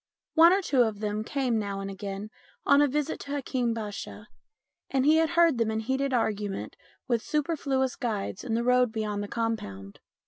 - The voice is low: No, high, 235 Hz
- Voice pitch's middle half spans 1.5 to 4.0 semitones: No, average, 4.8 semitones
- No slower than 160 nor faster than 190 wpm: Yes, average, 185 wpm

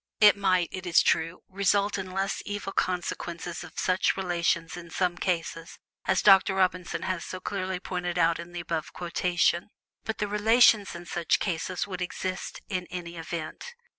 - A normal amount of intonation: No, narrow, 2.0 semitones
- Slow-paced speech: No, average, 165 wpm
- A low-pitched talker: No, medium, 180 Hz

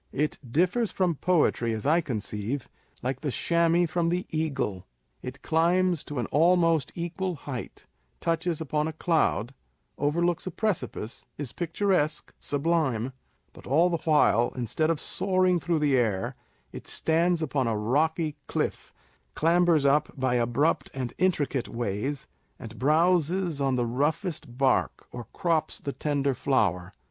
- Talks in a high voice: No, medium, 150 Hz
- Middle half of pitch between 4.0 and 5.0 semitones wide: Yes, average, 4.7 semitones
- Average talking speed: Yes, average, 145 wpm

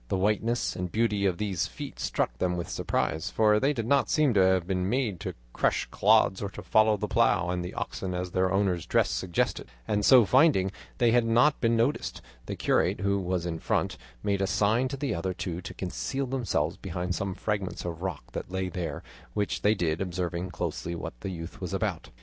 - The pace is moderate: No, fast, 210 wpm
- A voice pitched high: No, very low, 95 Hz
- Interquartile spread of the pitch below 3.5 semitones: No, average, 3.8 semitones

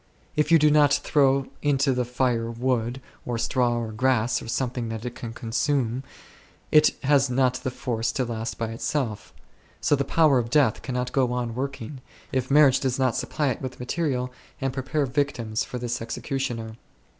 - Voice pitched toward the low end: Yes, low, 125 Hz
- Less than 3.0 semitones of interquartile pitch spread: Yes, narrow, 2.6 semitones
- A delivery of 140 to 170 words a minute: No, average, 180 wpm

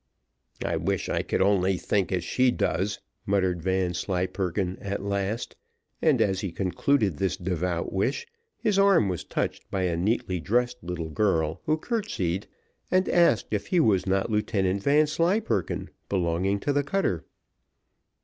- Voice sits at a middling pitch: No, very low, 95 Hz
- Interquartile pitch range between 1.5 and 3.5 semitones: No, average, 5.2 semitones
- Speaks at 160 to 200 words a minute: No, average, 145 wpm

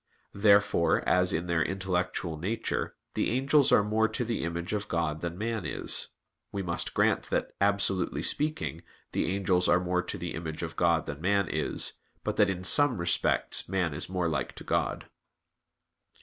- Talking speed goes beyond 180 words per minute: No, average, 175 wpm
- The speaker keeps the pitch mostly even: No, average, 3.2 semitones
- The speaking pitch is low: Yes, very low, 90 Hz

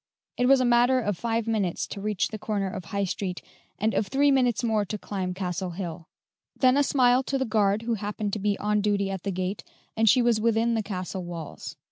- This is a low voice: No, high, 210 Hz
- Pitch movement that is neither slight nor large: Yes, average, 3.5 semitones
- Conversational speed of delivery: No, fast, 225 wpm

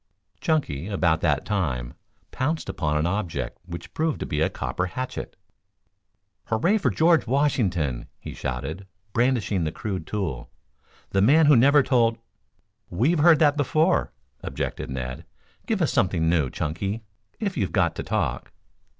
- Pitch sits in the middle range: No, low, 100 Hz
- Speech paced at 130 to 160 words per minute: Yes, average, 150 wpm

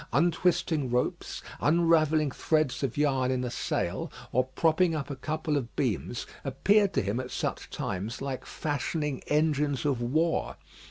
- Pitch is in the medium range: Yes, medium, 145 Hz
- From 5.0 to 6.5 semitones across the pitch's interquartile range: No, average, 3.6 semitones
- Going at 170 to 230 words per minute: No, average, 150 wpm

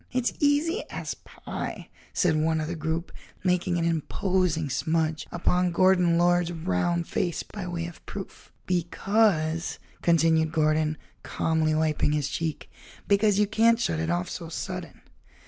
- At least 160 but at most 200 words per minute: No, average, 145 wpm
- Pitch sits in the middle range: Yes, medium, 170 Hz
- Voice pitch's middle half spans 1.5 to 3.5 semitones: Yes, narrow, 2.5 semitones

